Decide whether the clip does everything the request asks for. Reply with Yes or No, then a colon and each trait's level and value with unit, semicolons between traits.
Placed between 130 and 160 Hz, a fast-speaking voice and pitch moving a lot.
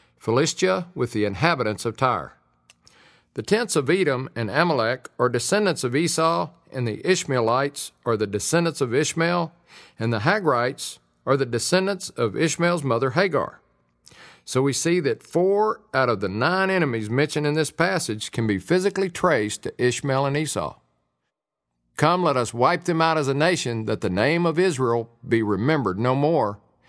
No: low, 135 Hz; average, 165 wpm; wide, 6.6 semitones